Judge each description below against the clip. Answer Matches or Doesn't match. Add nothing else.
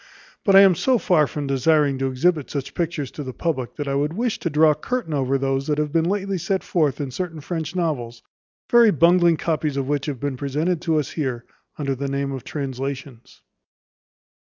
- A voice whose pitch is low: Doesn't match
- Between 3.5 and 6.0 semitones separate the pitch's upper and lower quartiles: Matches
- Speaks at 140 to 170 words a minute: Doesn't match